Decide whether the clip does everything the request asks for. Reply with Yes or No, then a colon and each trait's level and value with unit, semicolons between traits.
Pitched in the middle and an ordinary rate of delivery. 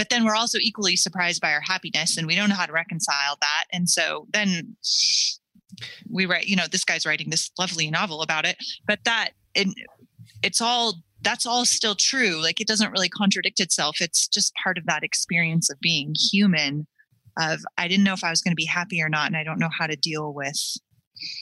No: medium, 180 Hz; fast, 215 wpm